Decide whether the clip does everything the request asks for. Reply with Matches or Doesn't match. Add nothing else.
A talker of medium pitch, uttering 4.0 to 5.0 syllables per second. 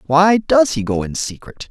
Matches